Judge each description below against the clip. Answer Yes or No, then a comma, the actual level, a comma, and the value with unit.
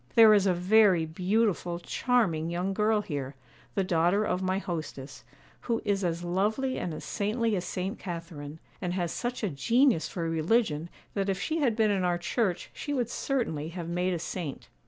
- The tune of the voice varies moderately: Yes, average, 4.4 semitones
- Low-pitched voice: No, medium, 185 Hz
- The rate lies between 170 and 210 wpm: Yes, average, 185 wpm